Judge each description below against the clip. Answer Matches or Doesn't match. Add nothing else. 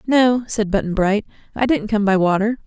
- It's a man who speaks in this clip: Doesn't match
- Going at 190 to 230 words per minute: Matches